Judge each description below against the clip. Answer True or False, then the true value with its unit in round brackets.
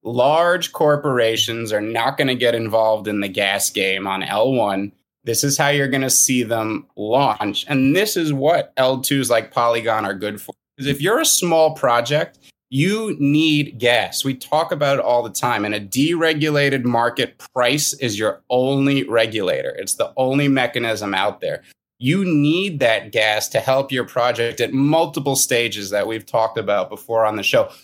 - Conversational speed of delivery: True (180 wpm)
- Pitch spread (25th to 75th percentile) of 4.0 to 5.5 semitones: True (4.6 semitones)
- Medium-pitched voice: False (130 Hz)